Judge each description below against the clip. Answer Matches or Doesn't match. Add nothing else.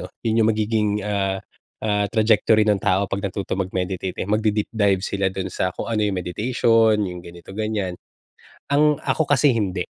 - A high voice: Doesn't match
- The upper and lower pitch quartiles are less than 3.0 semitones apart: Matches